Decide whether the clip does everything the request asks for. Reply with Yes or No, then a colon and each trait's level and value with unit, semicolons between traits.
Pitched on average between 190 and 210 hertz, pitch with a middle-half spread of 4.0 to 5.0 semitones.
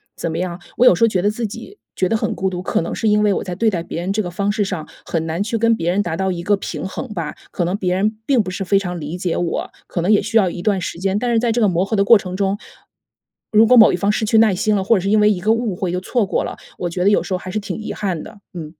No: high, 195 Hz; average, 3.2 semitones